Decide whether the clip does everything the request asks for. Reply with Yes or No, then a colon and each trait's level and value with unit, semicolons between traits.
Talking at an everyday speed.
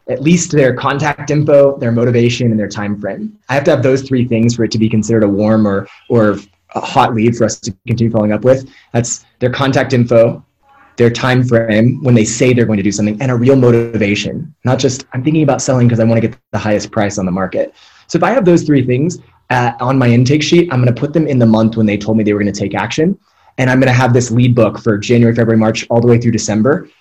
No: fast, 265 wpm